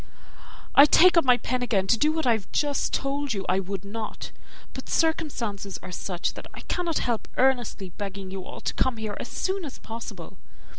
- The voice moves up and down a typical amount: No, wide, 6.4 semitones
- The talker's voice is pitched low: No, high, 235 Hz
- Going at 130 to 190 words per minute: No, average, 200 wpm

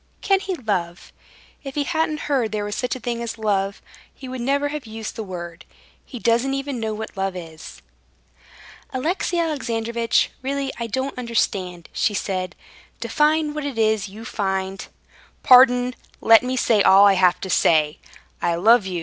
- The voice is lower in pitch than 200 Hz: No, high, 230 Hz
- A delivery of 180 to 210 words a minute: No, average, 170 wpm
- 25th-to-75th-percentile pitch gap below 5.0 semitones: No, wide, 5.5 semitones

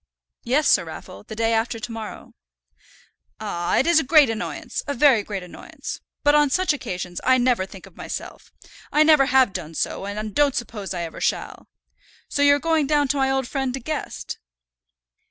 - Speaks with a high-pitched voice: Yes, very high, 250 Hz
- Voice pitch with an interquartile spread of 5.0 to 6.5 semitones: Yes, wide, 5.6 semitones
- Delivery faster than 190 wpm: No, average, 185 wpm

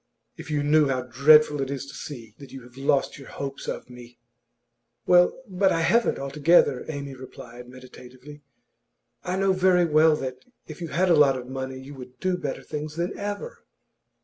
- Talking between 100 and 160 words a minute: No, average, 185 wpm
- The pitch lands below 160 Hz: Yes, medium, 140 Hz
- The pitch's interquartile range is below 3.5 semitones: No, average, 4.2 semitones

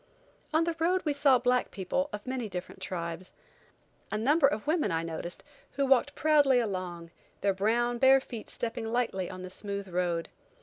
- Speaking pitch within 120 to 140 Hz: No, high, 225 Hz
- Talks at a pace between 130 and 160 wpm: No, average, 175 wpm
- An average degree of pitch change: No, wide, 6.7 semitones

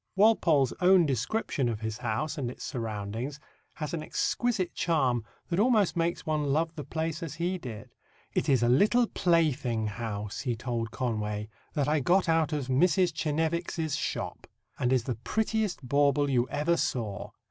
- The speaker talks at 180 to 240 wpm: No, average, 165 wpm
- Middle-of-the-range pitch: Yes, medium, 145 Hz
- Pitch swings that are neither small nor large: No, wide, 5.8 semitones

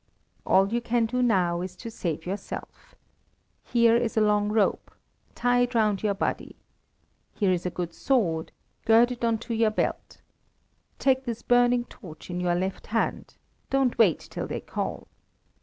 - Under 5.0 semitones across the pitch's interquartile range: Yes, average, 4.5 semitones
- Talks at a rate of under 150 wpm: No, average, 165 wpm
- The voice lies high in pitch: Yes, high, 220 Hz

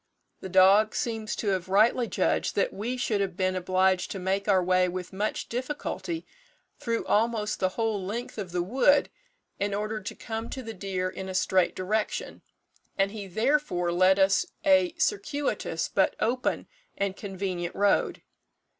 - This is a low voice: No, high, 200 Hz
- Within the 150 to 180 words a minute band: Yes, average, 165 wpm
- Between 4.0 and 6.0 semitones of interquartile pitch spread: No, average, 3.5 semitones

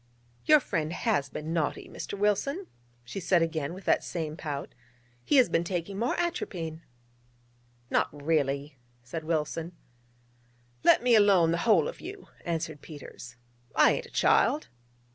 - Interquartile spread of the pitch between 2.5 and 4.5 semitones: No, average, 5.0 semitones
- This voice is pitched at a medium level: Yes, medium, 165 Hz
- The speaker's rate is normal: Yes, average, 145 wpm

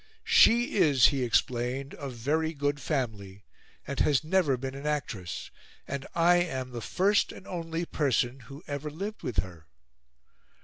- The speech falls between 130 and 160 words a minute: Yes, average, 150 wpm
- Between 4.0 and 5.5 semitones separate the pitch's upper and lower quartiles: Yes, average, 4.7 semitones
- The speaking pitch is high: No, medium, 140 Hz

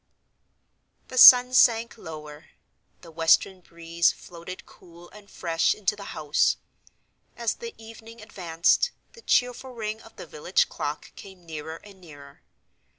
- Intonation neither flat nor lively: No, wide, 5.7 semitones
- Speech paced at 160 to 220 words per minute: No, slow, 135 wpm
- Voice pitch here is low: No, high, 190 Hz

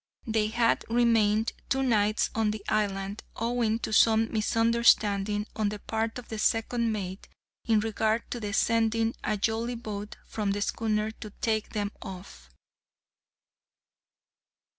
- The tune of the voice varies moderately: No, narrow, 1.5 semitones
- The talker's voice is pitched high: Yes, high, 220 Hz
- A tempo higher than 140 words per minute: No, slow, 135 wpm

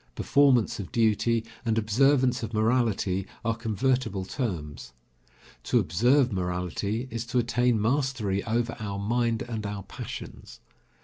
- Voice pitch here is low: Yes, low, 115 Hz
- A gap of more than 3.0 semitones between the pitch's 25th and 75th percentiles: Yes, average, 3.4 semitones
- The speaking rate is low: Yes, slow, 125 wpm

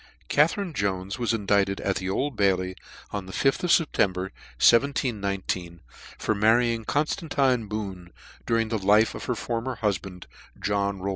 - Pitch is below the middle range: Yes, low, 105 Hz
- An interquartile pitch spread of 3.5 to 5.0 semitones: Yes, average, 3.9 semitones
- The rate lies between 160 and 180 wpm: No, average, 150 wpm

